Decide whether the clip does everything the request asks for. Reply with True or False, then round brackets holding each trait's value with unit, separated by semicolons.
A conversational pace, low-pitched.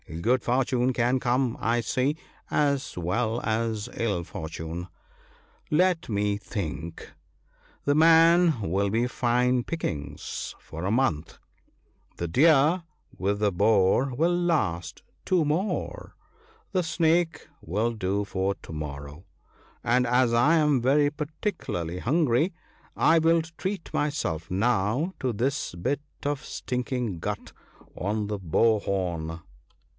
False (130 wpm; 120 Hz)